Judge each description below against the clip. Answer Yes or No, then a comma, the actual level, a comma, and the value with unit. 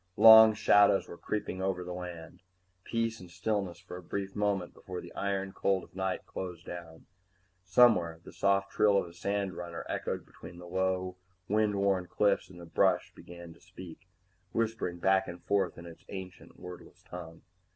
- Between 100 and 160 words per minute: No, average, 170 wpm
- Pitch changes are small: Yes, narrow, 2.2 semitones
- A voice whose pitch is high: No, very low, 95 Hz